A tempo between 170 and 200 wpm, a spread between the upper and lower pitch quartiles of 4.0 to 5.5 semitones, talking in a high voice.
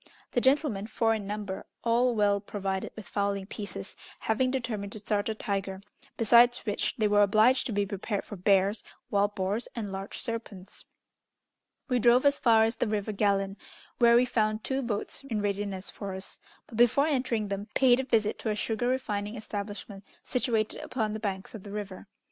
No: average, 185 wpm; average, 2.7 semitones; high, 215 Hz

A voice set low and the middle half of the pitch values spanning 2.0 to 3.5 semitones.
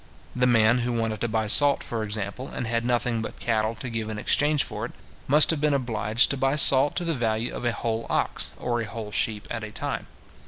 Yes: low, 115 Hz; average, 2.8 semitones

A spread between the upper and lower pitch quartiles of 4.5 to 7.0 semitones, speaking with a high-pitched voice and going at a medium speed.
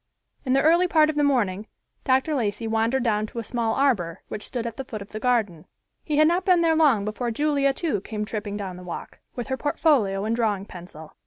No: wide, 5.5 semitones; high, 230 Hz; fast, 230 wpm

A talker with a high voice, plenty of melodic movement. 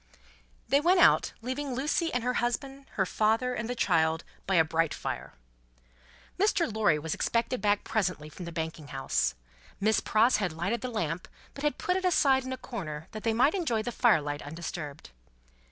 Yes: high, 220 Hz; wide, 8.0 semitones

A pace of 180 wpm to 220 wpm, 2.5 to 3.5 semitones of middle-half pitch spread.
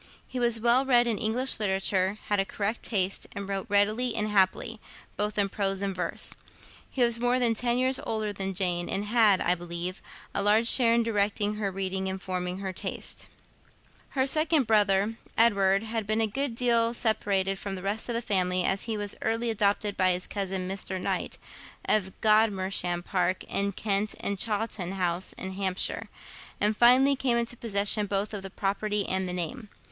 Yes: average, 185 wpm; average, 3.0 semitones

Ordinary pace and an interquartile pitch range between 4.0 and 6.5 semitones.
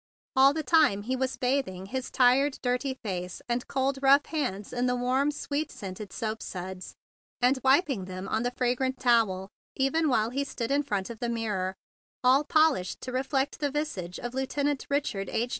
Yes: average, 185 wpm; average, 4.6 semitones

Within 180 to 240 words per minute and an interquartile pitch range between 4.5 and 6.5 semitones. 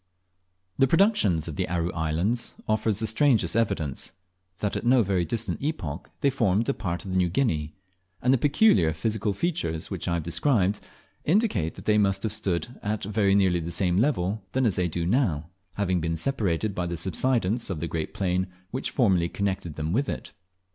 Yes: average, 190 wpm; average, 5.3 semitones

